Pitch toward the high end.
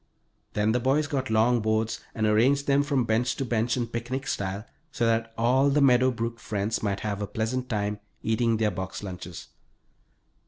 No: low, 115 Hz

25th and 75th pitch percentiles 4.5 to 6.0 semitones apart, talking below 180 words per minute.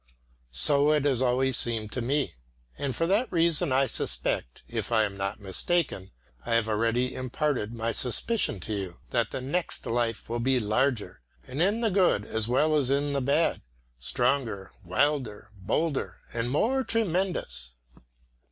Yes: wide, 5.4 semitones; average, 160 wpm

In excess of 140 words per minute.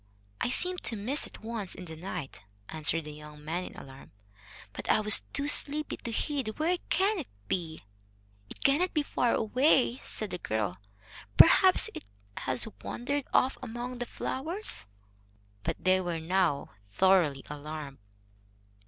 Yes: average, 155 wpm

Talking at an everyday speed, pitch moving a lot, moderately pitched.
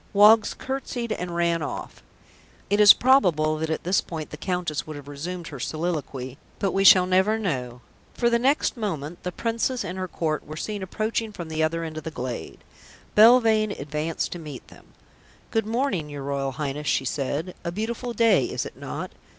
Yes: average, 190 wpm; wide, 6.0 semitones; medium, 175 Hz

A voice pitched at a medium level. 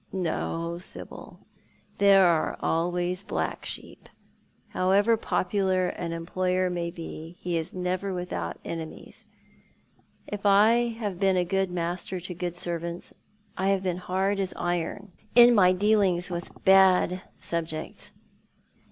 Yes: medium, 180 Hz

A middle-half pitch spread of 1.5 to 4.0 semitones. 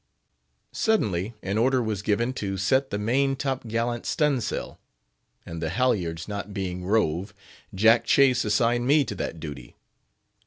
No: average, 4.8 semitones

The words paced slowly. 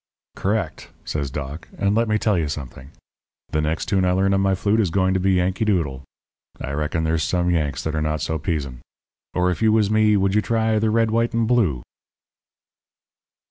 No: fast, 205 wpm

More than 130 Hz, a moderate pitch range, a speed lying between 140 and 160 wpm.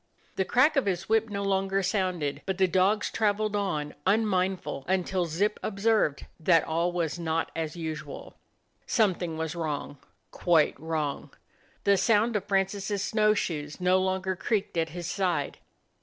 Yes: medium, 185 Hz; average, 3.6 semitones; average, 155 wpm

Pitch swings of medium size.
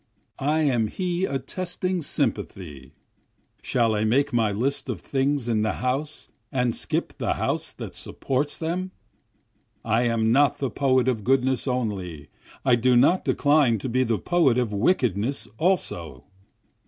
Yes: average, 4.4 semitones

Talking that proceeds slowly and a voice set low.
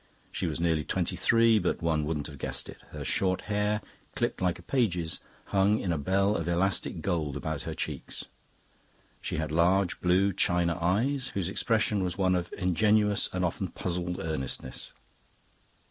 No: average, 165 wpm; very low, 90 Hz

